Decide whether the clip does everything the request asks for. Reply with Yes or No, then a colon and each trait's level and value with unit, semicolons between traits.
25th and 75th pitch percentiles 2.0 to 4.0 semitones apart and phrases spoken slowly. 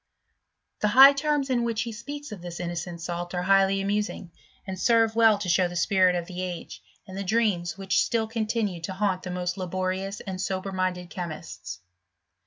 No: average, 3.5 semitones; average, 190 wpm